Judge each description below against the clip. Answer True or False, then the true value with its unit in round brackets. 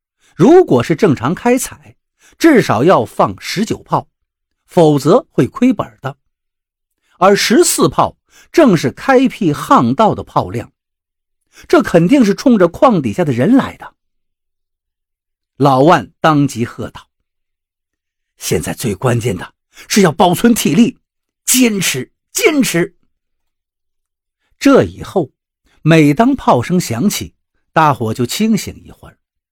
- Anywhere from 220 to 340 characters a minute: False (175 characters per minute)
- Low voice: False (170 Hz)